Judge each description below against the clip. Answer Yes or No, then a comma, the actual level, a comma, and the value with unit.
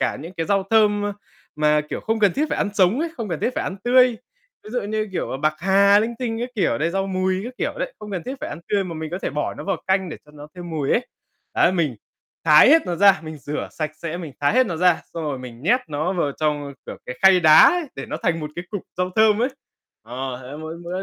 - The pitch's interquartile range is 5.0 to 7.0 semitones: Yes, average, 5.3 semitones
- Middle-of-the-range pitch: Yes, medium, 180 Hz